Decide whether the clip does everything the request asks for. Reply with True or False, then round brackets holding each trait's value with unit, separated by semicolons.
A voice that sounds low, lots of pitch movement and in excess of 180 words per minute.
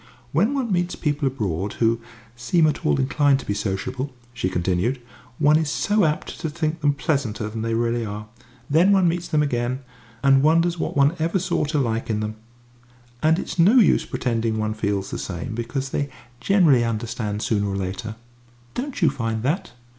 True (130 Hz; 6.2 semitones; 190 wpm)